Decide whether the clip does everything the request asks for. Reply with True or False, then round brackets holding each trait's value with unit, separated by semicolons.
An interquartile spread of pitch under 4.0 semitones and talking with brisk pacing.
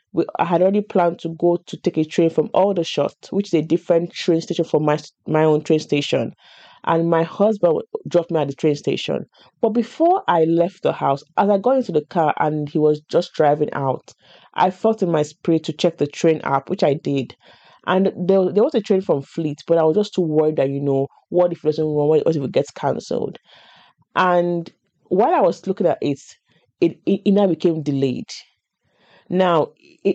True (3.5 semitones; 210 wpm)